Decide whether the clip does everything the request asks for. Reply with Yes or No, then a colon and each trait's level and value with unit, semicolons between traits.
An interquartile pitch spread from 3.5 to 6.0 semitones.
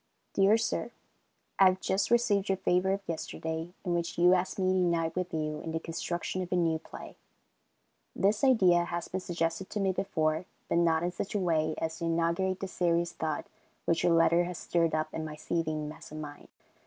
No: narrow, 2.5 semitones